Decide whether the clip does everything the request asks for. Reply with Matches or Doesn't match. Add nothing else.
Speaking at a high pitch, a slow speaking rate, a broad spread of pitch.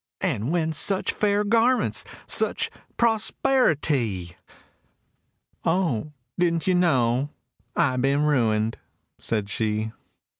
Doesn't match